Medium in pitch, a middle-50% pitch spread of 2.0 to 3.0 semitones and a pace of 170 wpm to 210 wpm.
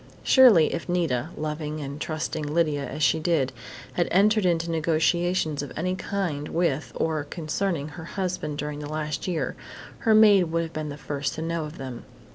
Yes: medium, 160 Hz; average, 2.7 semitones; average, 180 wpm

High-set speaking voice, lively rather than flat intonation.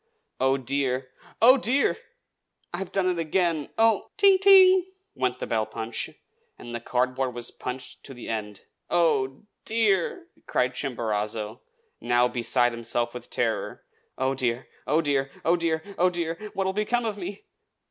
No: low, 135 Hz; wide, 7.7 semitones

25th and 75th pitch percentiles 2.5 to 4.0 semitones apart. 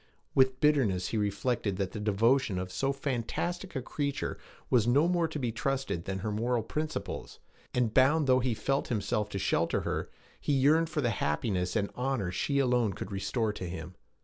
No: average, 5.1 semitones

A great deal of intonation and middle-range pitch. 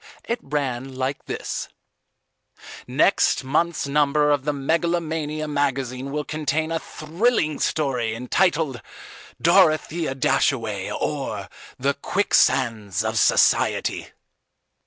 No: average, 3.0 semitones; medium, 145 Hz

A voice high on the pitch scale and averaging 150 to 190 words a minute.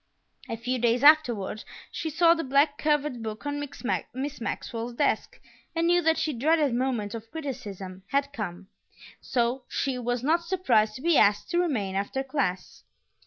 Yes: very high, 260 Hz; average, 165 wpm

